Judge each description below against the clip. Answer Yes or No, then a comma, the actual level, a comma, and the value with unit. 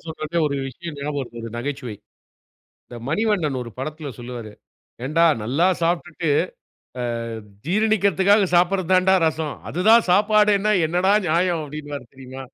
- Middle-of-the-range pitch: Yes, medium, 165 Hz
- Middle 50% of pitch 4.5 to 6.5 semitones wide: Yes, average, 5.1 semitones